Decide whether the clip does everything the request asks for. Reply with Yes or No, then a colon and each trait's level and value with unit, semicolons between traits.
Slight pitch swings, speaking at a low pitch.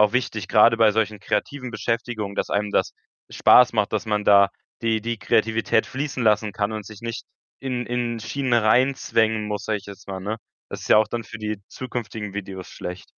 Yes: narrow, 2.1 semitones; low, 110 Hz